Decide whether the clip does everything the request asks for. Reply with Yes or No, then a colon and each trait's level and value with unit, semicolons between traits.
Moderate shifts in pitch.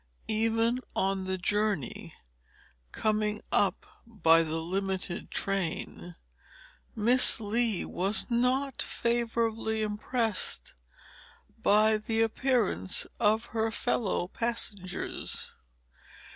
Yes: average, 3.1 semitones